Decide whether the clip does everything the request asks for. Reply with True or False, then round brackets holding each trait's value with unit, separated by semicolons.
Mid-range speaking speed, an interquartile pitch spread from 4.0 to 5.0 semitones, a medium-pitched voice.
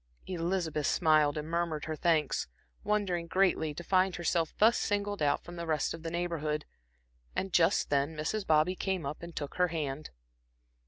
False (170 wpm; 2.9 semitones; 165 Hz)